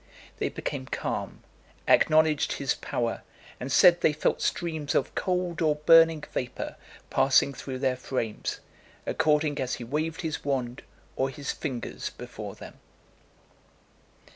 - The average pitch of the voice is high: No, medium, 145 Hz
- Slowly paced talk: Yes, slow, 130 wpm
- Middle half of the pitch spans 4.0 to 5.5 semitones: No, average, 3.5 semitones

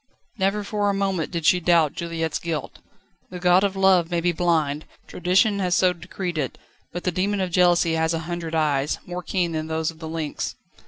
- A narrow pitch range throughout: Yes, narrow, 2.3 semitones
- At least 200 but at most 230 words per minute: Yes, fast, 205 wpm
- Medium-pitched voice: Yes, medium, 175 Hz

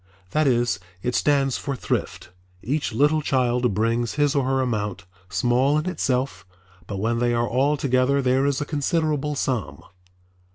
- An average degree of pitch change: Yes, average, 3.3 semitones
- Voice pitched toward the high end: No, low, 130 Hz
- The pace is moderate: Yes, average, 160 wpm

